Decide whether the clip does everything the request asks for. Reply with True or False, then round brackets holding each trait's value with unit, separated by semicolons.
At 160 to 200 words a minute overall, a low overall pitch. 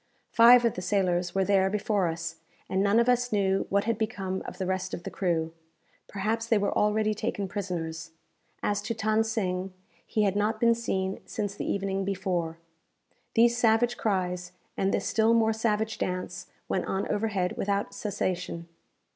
False (170 wpm; 200 Hz)